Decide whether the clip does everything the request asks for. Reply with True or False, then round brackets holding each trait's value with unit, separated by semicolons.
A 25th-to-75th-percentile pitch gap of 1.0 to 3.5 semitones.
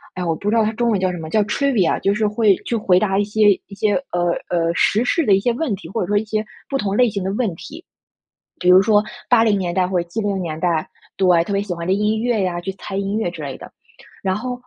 True (3.2 semitones)